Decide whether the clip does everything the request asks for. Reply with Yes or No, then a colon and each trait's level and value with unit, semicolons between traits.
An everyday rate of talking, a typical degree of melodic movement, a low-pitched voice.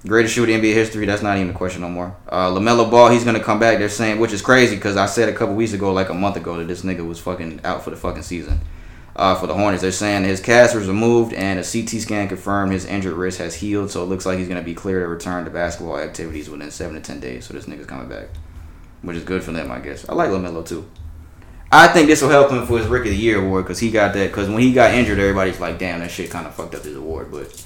No: fast, 295 wpm; average, 4.1 semitones; very low, 95 Hz